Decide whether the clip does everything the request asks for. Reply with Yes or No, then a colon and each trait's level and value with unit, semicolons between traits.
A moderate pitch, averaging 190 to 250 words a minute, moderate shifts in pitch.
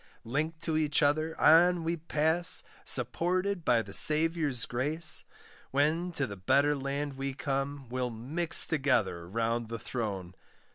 No: medium, 145 Hz; average, 140 wpm; average, 4.6 semitones